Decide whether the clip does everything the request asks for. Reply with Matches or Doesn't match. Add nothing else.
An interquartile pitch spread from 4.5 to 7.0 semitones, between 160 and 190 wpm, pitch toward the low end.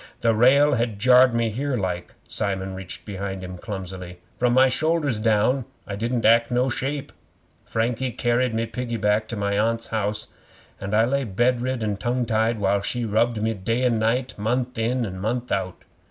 Doesn't match